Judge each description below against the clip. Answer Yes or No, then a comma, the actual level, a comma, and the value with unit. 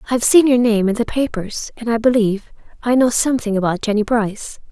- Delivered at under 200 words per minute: No, fast, 205 wpm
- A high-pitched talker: Yes, high, 230 Hz